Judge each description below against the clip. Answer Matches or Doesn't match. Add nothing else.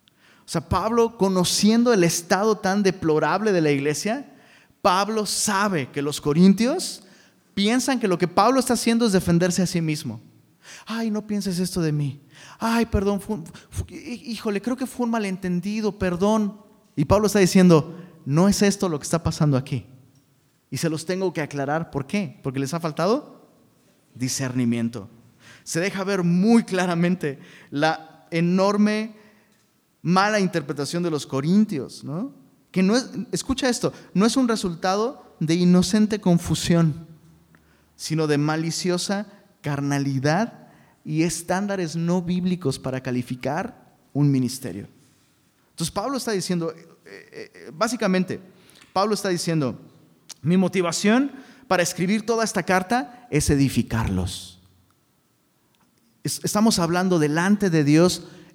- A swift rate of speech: Doesn't match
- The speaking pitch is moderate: Matches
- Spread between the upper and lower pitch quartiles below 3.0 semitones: Doesn't match